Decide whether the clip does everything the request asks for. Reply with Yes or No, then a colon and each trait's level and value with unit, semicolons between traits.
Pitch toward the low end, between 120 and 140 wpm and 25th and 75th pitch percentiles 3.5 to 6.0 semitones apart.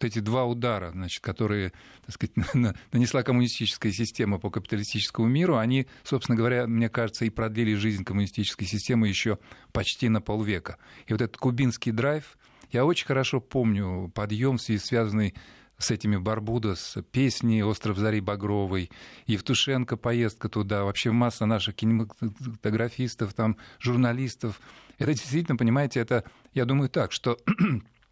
No: low, 115 Hz; average, 135 wpm; average, 2.8 semitones